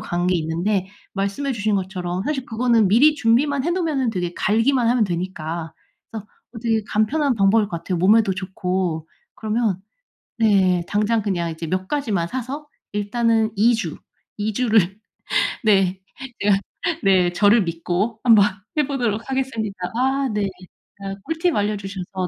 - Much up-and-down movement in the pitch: No, average, 4.2 semitones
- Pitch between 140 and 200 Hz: No, high, 210 Hz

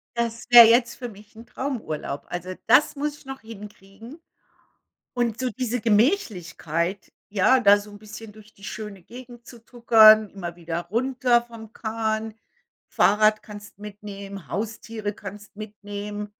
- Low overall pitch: No, high, 215 Hz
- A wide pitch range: No, narrow, 2.6 semitones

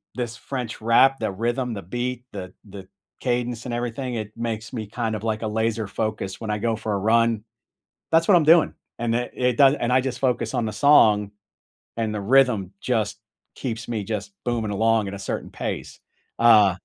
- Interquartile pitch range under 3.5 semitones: Yes, narrow, 2.6 semitones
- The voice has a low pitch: Yes, low, 115 Hz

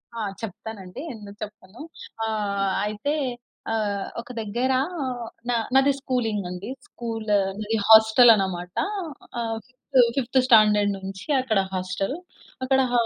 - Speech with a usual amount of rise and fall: Yes, average, 3.0 semitones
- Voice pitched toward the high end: Yes, high, 215 Hz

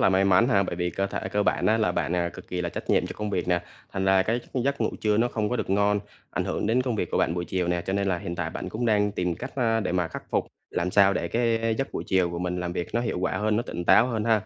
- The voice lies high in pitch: No, low, 100 Hz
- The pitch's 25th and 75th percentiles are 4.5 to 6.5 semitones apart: No, average, 3.9 semitones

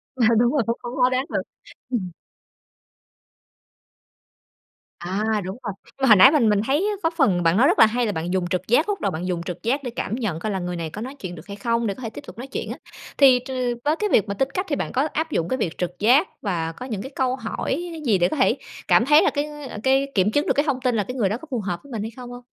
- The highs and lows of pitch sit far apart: Yes, wide, 5.8 semitones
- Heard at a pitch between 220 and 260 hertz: Yes, high, 235 Hz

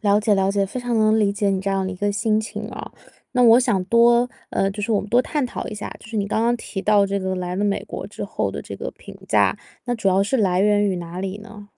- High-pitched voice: Yes, high, 205 Hz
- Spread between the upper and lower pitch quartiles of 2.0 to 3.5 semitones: Yes, narrow, 2.4 semitones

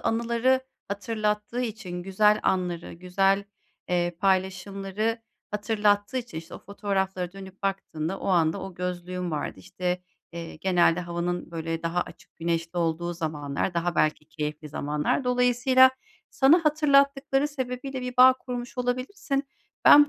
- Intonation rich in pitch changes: Yes, wide, 6.0 semitones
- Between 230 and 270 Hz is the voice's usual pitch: No, high, 195 Hz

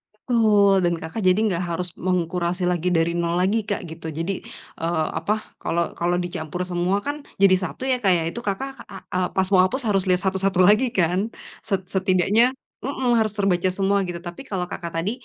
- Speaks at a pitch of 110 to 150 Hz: No, medium, 185 Hz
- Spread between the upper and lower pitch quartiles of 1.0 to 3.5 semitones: Yes, average, 2.8 semitones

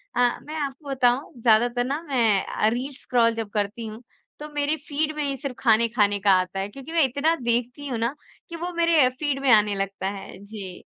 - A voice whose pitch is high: Yes, high, 245 Hz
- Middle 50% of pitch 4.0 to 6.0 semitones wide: Yes, average, 4.8 semitones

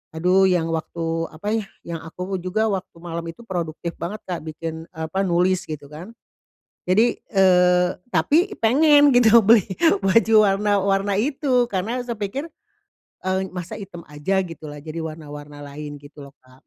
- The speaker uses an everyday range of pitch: Yes, average, 4.5 semitones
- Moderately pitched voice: Yes, medium, 180 Hz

